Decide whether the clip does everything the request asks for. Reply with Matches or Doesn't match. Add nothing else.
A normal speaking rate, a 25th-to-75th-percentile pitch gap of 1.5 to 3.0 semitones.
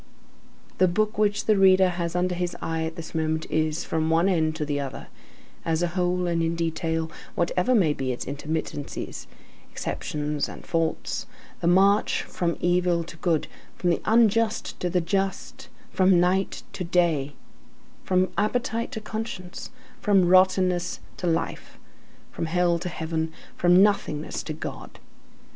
Matches